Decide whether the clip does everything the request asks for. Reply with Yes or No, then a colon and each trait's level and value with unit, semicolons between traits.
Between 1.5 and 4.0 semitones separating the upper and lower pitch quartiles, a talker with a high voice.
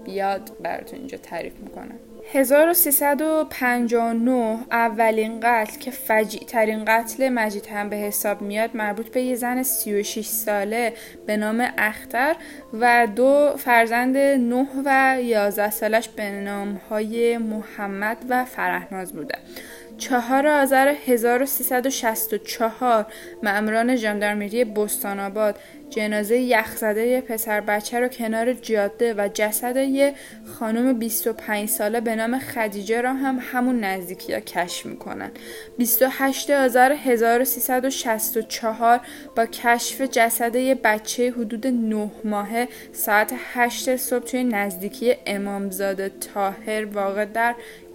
Yes: average, 3.0 semitones; high, 230 Hz